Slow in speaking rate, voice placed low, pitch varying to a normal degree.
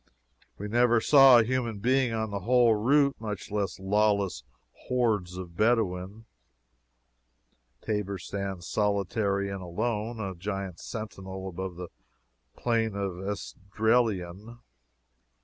Yes: slow, 115 wpm; low, 105 Hz; average, 3.1 semitones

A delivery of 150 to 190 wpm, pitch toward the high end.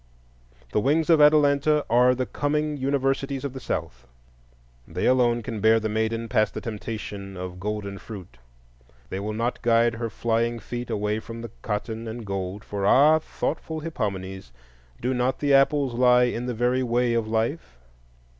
No: average, 160 wpm; low, 115 Hz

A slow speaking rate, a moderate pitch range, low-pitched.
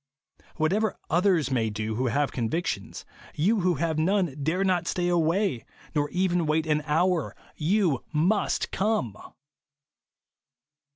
No: slow, 125 wpm; average, 4.0 semitones; medium, 165 Hz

